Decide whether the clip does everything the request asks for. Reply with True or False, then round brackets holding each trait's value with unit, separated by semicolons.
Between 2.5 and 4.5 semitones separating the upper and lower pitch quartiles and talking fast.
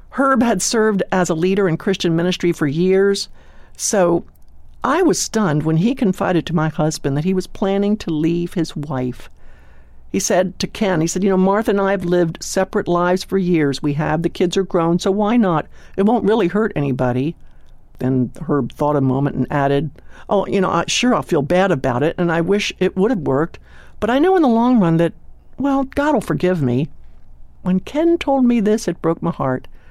False (5.0 semitones; 215 wpm)